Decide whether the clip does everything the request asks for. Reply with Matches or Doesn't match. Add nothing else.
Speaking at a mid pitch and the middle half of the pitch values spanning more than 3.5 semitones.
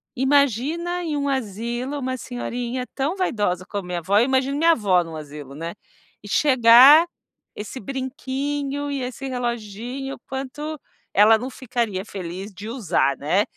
Doesn't match